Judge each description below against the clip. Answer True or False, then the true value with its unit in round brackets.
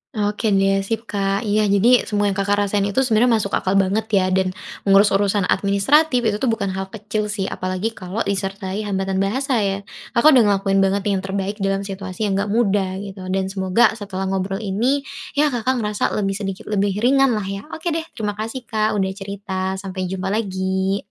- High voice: True (200 Hz)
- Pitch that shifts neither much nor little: False (2.0 semitones)